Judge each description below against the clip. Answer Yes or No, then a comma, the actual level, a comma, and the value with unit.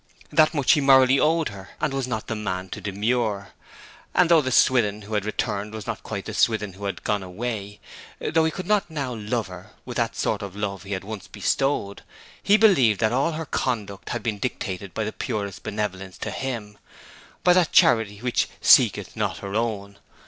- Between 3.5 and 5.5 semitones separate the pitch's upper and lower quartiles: Yes, average, 5.0 semitones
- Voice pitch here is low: Yes, low, 110 Hz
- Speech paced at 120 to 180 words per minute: No, average, 200 wpm